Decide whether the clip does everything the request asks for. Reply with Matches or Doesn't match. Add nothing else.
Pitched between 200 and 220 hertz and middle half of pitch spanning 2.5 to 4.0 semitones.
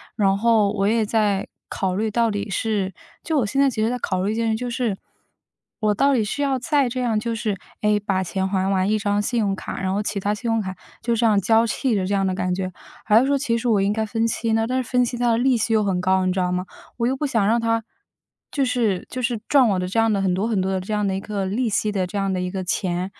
Matches